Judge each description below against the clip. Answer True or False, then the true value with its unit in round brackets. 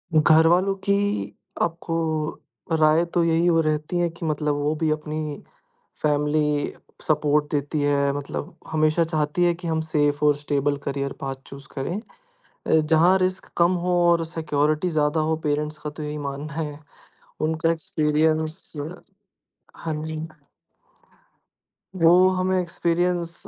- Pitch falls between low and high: True (155 Hz)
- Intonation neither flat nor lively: False (2.0 semitones)